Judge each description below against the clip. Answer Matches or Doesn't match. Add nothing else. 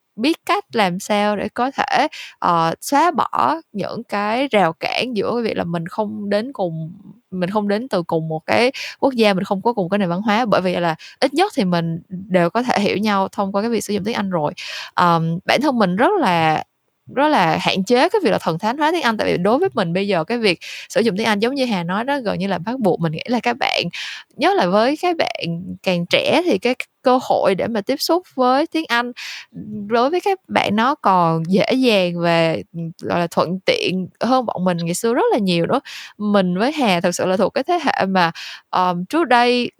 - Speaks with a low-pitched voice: Doesn't match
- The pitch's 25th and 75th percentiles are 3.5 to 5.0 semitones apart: Doesn't match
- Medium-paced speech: Matches